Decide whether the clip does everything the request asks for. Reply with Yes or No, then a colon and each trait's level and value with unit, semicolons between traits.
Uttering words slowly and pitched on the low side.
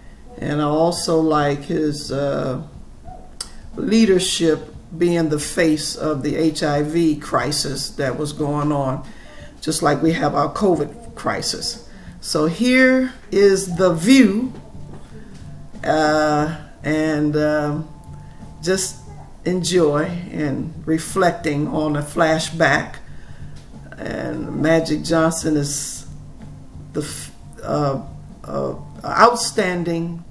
No: slow, 95 wpm; medium, 155 Hz